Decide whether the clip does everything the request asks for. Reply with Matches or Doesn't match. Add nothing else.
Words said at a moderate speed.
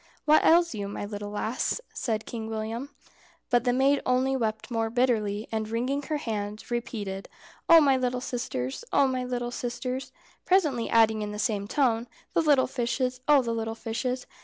Matches